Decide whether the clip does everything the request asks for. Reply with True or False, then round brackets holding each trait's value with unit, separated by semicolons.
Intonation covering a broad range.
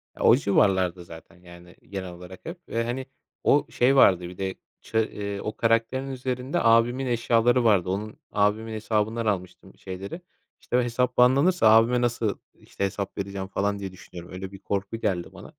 False (4.2 semitones)